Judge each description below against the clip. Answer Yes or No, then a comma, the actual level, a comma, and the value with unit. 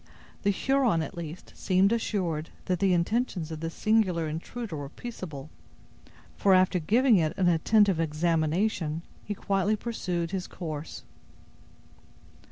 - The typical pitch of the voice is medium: Yes, medium, 180 Hz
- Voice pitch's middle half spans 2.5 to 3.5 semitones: No, average, 4.3 semitones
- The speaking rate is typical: No, slow, 130 wpm